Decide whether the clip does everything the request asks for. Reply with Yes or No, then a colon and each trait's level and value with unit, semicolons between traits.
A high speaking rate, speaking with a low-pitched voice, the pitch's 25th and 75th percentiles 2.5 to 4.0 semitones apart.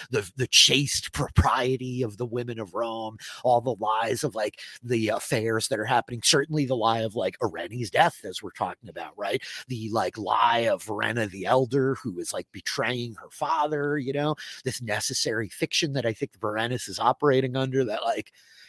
No: average, 185 wpm; low, 120 Hz; average, 3.2 semitones